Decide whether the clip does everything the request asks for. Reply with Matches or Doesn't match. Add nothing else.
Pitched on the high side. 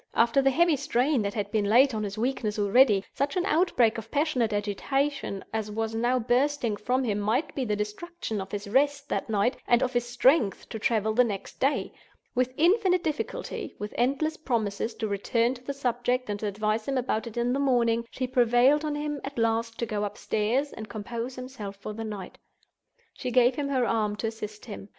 Matches